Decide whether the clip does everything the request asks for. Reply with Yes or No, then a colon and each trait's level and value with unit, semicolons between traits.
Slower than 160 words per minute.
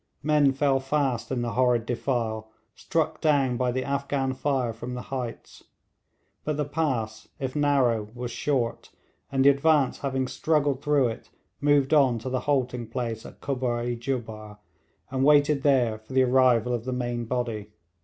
No: average, 165 wpm